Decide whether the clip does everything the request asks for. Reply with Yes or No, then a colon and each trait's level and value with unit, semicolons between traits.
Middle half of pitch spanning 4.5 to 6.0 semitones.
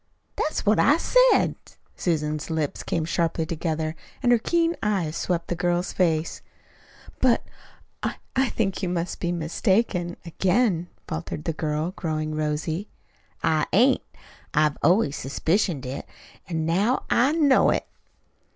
Yes: average, 5.1 semitones